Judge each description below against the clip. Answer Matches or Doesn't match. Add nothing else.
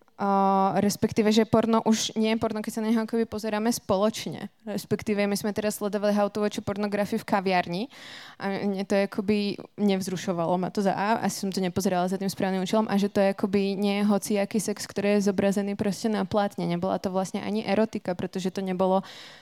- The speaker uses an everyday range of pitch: Doesn't match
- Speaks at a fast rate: Matches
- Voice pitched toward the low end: Doesn't match